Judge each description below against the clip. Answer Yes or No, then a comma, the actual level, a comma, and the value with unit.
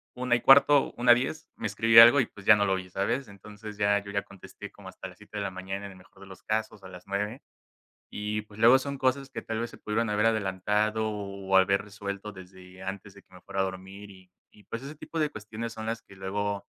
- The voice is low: Yes, low, 105 Hz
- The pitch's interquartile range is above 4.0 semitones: No, average, 2.7 semitones